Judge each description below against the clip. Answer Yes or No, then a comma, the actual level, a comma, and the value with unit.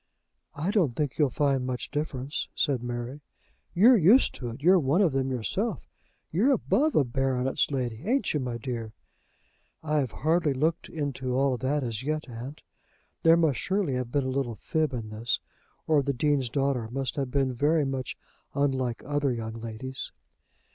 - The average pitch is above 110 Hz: Yes, low, 135 Hz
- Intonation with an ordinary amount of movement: Yes, average, 3.4 semitones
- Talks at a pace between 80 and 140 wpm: No, average, 175 wpm